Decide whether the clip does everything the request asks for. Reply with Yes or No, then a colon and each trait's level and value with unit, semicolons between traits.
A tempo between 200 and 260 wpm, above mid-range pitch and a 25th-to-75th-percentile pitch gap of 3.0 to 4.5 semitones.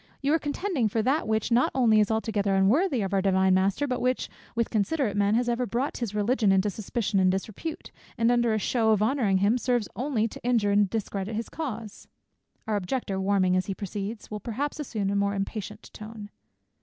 Yes: fast, 205 wpm; high, 215 Hz; average, 3.4 semitones